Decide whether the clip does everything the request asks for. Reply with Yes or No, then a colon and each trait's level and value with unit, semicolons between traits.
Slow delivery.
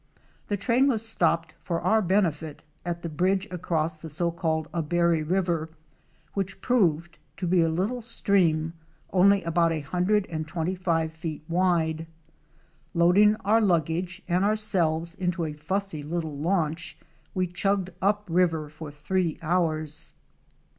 No: average, 145 wpm